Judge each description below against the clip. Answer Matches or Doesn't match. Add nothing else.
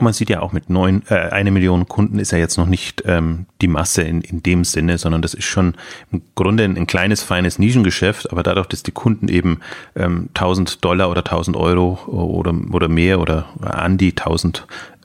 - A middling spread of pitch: Doesn't match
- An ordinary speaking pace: Doesn't match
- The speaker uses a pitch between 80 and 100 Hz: Matches